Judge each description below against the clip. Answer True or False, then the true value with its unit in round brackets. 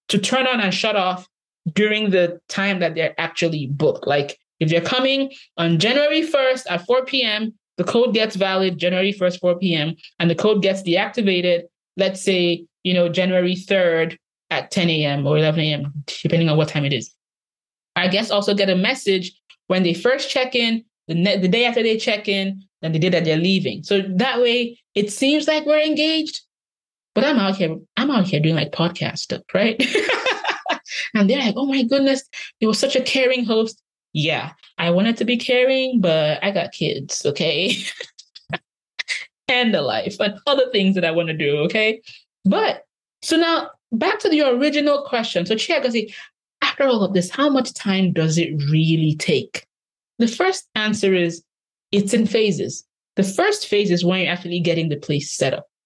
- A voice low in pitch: False (195 Hz)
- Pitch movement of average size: False (6.1 semitones)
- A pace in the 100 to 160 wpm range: False (185 wpm)